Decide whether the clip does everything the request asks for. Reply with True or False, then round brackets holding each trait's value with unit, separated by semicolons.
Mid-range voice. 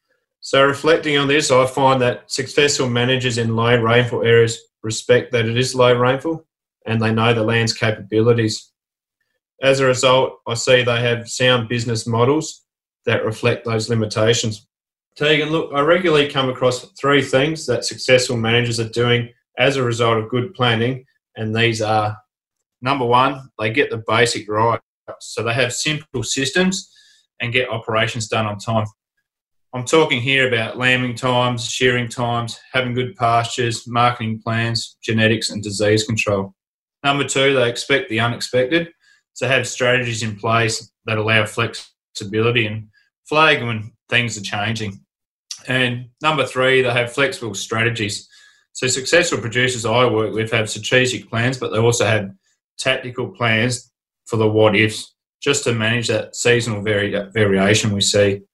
False (120 Hz)